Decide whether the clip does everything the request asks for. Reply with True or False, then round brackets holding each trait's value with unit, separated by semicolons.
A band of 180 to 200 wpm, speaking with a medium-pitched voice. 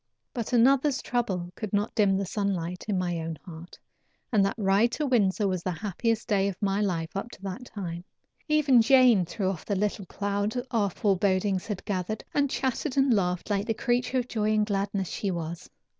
False (195 wpm; 205 Hz)